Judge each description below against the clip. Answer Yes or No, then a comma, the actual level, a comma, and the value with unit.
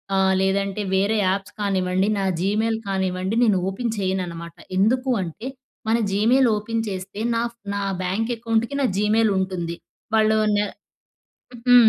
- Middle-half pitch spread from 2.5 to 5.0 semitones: Yes, average, 2.9 semitones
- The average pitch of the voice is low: No, high, 200 Hz